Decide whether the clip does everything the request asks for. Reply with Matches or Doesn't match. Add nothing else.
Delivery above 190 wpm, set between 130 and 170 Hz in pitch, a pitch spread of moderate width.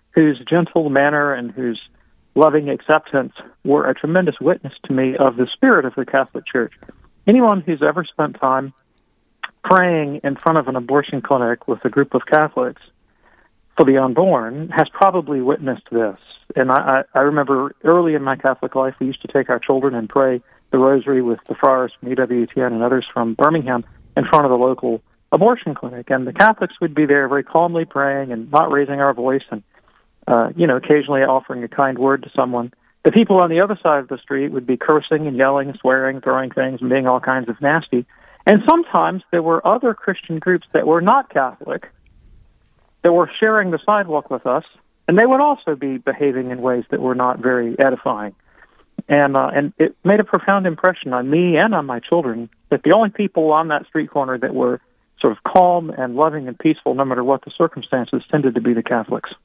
Matches